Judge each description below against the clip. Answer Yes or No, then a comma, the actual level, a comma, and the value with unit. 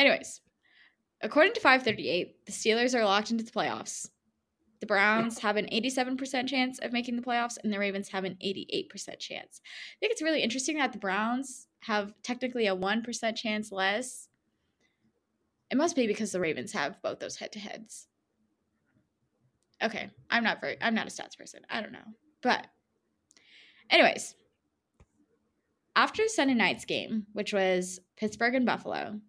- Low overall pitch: No, high, 225 Hz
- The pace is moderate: Yes, average, 155 wpm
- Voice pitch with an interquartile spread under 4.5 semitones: Yes, average, 3.5 semitones